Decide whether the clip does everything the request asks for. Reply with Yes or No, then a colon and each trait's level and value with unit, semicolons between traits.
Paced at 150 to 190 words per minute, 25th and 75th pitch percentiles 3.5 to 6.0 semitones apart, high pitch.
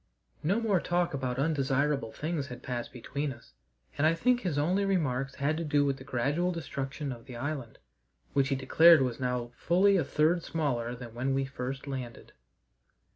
No: average, 180 wpm; average, 4.2 semitones; medium, 140 Hz